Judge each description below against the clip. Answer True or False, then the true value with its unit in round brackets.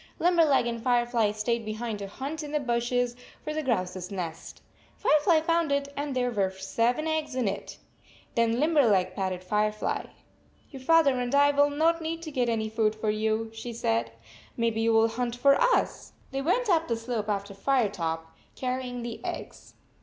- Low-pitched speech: False (240 Hz)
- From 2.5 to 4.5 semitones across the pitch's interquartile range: False (5.0 semitones)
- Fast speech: False (185 wpm)